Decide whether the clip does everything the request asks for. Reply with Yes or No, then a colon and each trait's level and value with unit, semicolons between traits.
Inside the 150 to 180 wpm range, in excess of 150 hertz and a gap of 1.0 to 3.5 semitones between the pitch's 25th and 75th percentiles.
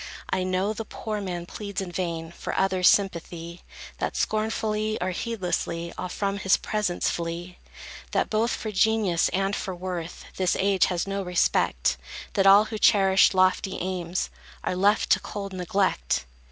Yes: average, 155 wpm; high, 190 Hz; narrow, 2.5 semitones